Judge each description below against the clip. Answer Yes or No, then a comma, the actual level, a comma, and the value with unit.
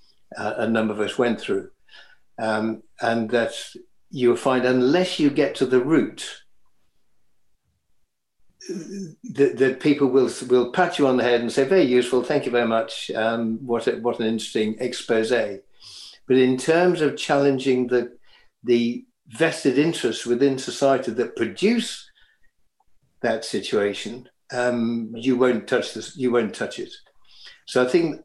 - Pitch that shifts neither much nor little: Yes, average, 3.8 semitones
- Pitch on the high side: No, low, 125 Hz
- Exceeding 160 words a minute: No, average, 150 wpm